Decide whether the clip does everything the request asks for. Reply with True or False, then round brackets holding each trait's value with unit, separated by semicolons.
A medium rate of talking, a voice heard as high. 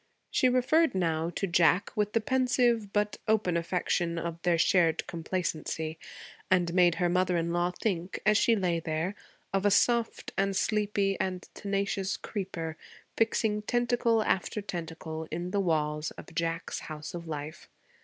False (155 wpm; 180 Hz)